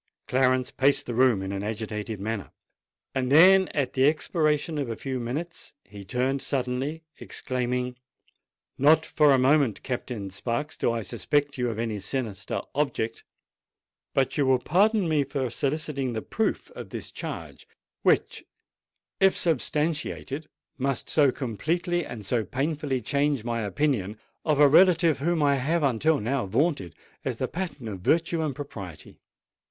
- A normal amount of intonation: Yes, average, 4.5 semitones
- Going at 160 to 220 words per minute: No, average, 150 wpm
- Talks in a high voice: No, low, 135 Hz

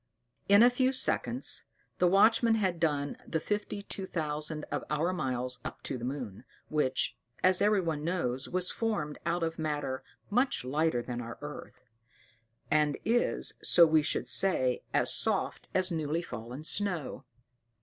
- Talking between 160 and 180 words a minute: No, average, 150 wpm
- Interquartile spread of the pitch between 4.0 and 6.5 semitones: Yes, average, 5.1 semitones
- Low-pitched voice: No, medium, 160 Hz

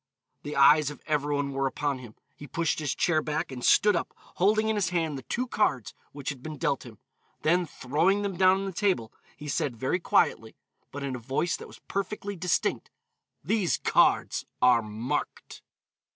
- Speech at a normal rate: Yes, average, 190 wpm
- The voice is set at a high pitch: No, medium, 150 Hz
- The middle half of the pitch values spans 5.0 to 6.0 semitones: Yes, wide, 5.5 semitones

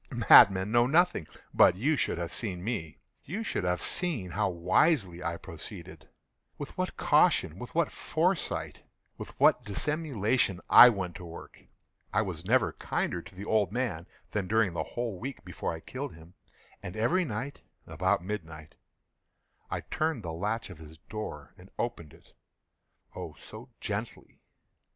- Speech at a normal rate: Yes, average, 145 wpm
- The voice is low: Yes, low, 100 Hz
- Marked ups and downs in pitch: Yes, wide, 5.7 semitones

